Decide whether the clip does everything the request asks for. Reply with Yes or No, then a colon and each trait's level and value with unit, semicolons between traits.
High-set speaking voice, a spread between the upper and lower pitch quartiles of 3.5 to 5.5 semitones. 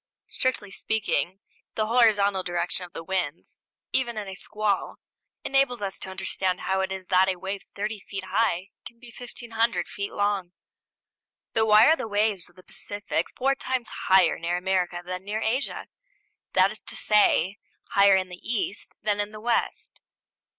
No: high, 200 Hz; average, 2.8 semitones